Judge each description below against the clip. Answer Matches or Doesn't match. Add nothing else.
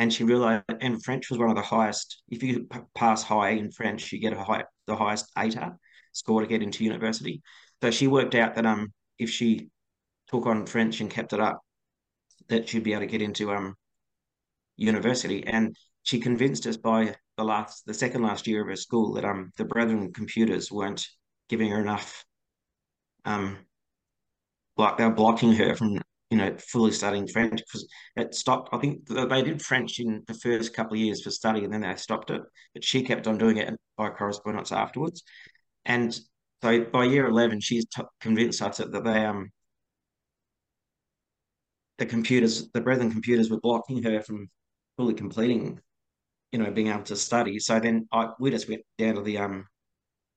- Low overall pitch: Matches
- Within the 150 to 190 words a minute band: Matches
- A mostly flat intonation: Matches